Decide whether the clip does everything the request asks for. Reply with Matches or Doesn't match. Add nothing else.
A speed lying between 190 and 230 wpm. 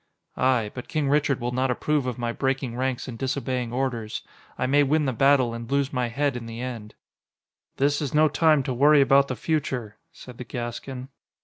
Matches